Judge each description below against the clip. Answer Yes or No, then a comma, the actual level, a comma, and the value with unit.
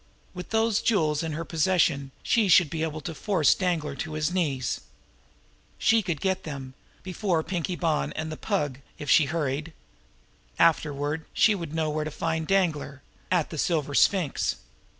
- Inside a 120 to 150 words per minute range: No, average, 165 wpm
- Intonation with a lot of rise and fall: No, average, 3.3 semitones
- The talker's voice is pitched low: No, medium, 160 Hz